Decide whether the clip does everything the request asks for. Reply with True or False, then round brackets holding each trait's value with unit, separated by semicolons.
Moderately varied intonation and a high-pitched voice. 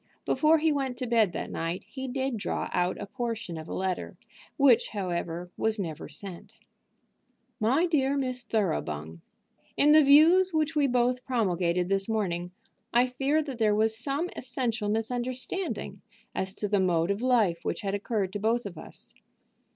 False (5.8 semitones; 225 Hz)